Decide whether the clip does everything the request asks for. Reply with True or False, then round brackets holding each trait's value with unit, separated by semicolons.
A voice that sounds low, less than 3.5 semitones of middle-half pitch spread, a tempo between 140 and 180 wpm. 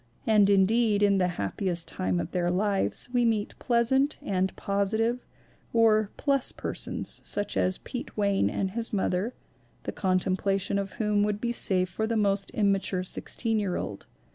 False (200 Hz; 2.9 semitones; 170 wpm)